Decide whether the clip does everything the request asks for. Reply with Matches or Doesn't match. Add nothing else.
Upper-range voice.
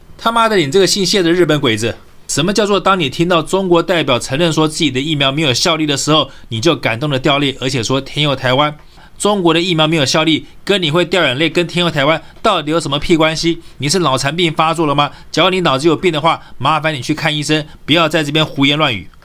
Doesn't match